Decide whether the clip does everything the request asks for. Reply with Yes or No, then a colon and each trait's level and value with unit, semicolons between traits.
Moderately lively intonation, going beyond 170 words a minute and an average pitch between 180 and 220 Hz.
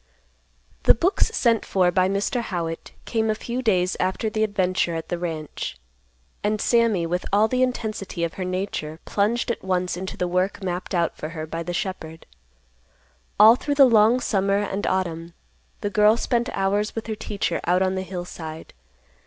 Yes: average, 3.6 semitones; average, 180 wpm; high, 190 Hz